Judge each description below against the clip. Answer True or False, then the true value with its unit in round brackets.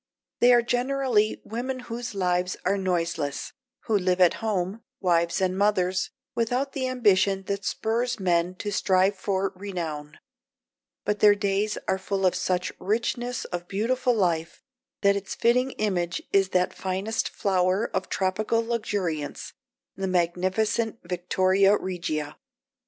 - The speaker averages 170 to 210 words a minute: False (135 wpm)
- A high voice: True (195 Hz)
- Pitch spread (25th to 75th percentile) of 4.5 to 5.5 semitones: False (3.4 semitones)